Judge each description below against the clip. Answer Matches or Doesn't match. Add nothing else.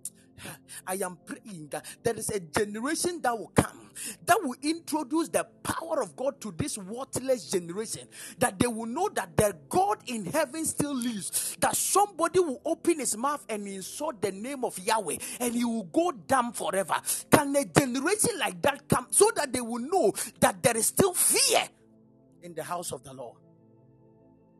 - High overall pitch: Matches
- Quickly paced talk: Doesn't match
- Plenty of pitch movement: Matches